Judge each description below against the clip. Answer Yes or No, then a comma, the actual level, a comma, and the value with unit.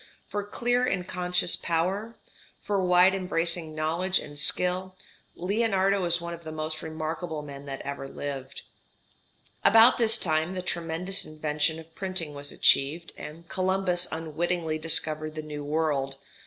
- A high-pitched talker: No, medium, 165 Hz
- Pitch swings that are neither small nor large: Yes, average, 3.2 semitones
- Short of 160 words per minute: Yes, average, 140 wpm